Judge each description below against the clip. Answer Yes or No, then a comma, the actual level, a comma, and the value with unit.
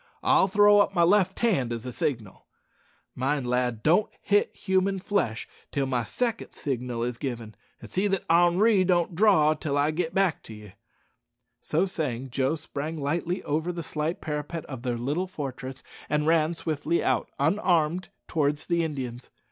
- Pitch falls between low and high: Yes, medium, 155 Hz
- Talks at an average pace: Yes, average, 165 wpm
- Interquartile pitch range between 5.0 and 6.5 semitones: Yes, wide, 5.4 semitones